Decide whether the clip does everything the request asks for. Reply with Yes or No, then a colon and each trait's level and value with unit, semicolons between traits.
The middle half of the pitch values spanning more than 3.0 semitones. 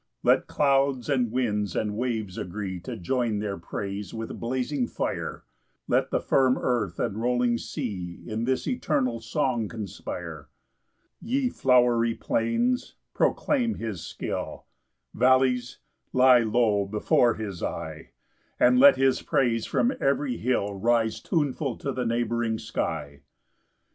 Yes: average, 3.4 semitones